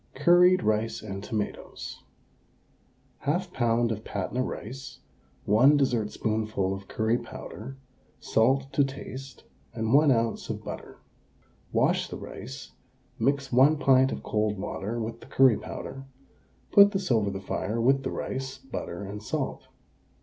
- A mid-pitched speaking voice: No, low, 120 Hz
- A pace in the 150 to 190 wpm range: No, slow, 135 wpm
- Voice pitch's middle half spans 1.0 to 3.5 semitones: No, average, 3.9 semitones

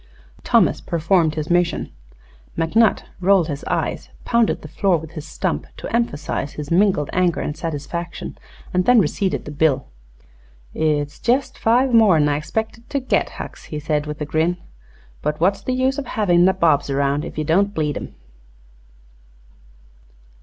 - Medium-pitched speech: Yes, medium, 170 Hz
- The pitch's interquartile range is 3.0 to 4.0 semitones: No, average, 5.1 semitones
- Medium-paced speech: Yes, average, 155 wpm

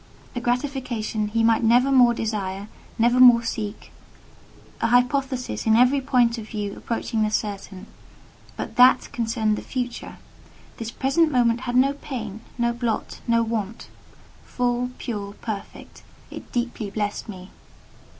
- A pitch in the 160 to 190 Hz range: No, high, 235 Hz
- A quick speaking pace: No, slow, 135 wpm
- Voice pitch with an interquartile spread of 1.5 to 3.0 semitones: Yes, narrow, 2.4 semitones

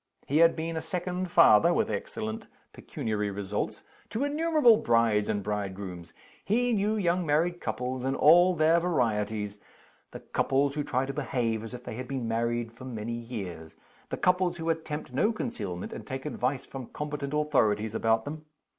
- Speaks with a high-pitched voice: No, low, 130 Hz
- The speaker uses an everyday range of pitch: No, wide, 7.1 semitones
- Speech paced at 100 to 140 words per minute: No, average, 170 wpm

